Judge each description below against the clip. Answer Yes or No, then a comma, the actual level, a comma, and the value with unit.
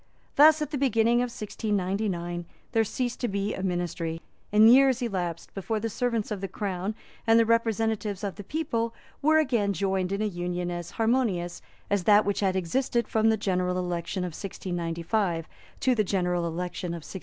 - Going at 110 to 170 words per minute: No, average, 180 wpm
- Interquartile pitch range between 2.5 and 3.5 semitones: No, average, 4.2 semitones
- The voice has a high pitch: Yes, high, 200 Hz